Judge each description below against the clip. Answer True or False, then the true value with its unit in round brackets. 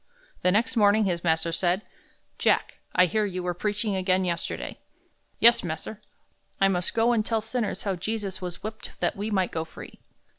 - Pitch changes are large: False (3.4 semitones)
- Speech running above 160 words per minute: True (180 wpm)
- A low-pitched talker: False (195 Hz)